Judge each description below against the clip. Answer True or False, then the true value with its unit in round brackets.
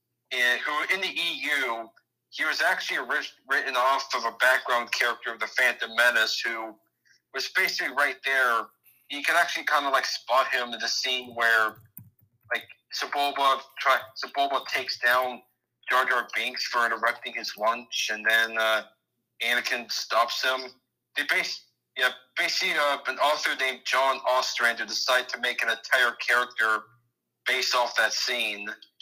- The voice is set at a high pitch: False (120 Hz)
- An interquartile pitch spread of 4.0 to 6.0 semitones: False (2.4 semitones)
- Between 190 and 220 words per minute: False (155 wpm)